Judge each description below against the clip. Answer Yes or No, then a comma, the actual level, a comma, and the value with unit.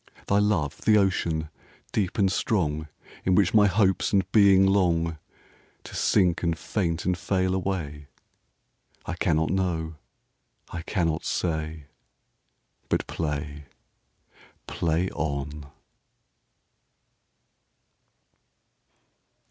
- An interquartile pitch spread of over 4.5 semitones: No, average, 3.6 semitones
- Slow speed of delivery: Yes, slow, 85 wpm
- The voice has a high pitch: No, very low, 85 Hz